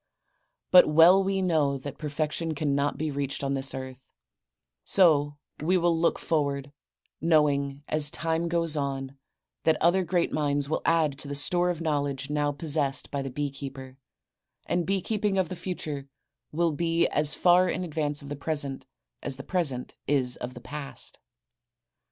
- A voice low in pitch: No, medium, 150 Hz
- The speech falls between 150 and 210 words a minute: Yes, average, 170 wpm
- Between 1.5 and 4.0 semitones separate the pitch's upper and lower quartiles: Yes, average, 3.1 semitones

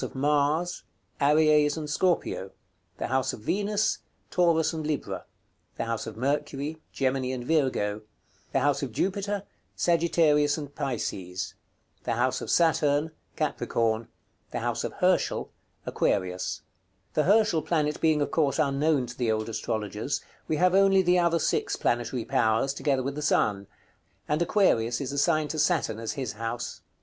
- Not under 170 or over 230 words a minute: No, average, 140 wpm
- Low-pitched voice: No, medium, 145 Hz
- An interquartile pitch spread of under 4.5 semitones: No, average, 5.1 semitones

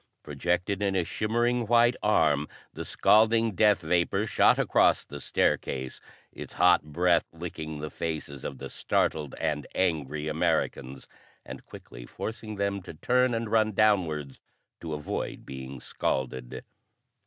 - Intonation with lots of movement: Yes, wide, 6.2 semitones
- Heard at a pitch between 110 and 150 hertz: No, very low, 85 Hz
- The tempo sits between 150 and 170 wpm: No, slow, 135 wpm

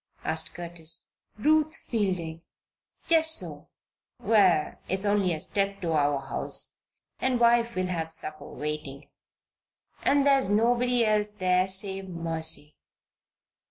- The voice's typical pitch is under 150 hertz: No, high, 190 Hz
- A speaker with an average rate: No, slow, 120 wpm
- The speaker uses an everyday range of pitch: No, wide, 6.3 semitones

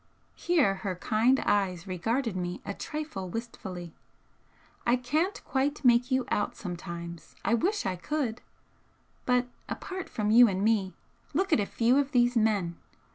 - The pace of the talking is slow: No, average, 150 wpm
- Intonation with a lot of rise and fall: Yes, wide, 5.8 semitones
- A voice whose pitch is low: No, high, 225 Hz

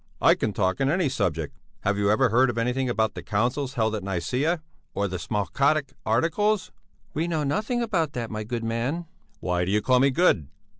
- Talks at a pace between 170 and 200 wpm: Yes, average, 195 wpm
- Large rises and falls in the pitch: Yes, wide, 5.9 semitones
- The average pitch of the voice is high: No, low, 120 Hz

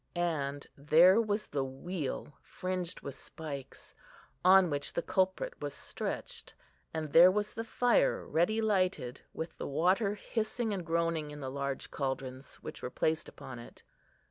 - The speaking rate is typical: Yes, average, 150 wpm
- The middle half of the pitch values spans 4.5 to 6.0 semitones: Yes, wide, 5.6 semitones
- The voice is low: No, medium, 170 Hz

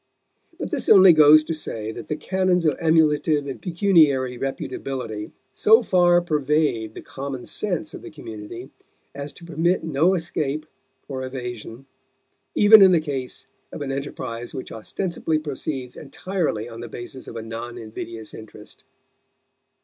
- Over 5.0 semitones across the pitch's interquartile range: Yes, wide, 5.4 semitones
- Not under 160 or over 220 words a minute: No, average, 150 wpm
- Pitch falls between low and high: Yes, medium, 145 Hz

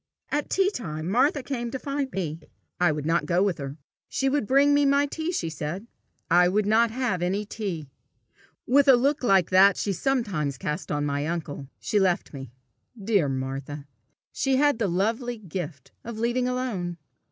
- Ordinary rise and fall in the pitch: No, wide, 7.7 semitones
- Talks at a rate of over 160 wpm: Yes, average, 180 wpm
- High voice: Yes, high, 200 Hz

